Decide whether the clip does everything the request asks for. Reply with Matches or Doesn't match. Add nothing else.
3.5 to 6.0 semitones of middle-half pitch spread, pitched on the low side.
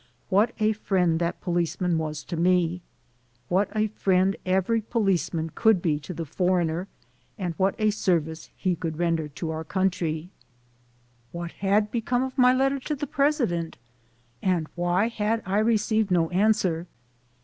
Doesn't match